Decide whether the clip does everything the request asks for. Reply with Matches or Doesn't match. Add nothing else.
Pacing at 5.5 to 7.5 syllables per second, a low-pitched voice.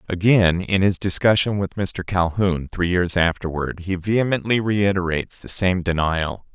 Doesn't match